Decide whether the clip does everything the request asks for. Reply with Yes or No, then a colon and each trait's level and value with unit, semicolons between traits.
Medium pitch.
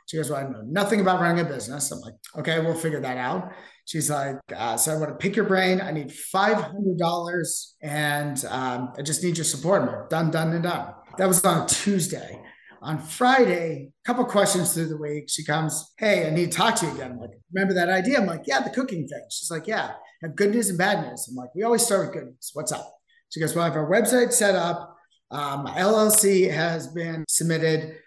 Yes: medium, 170 Hz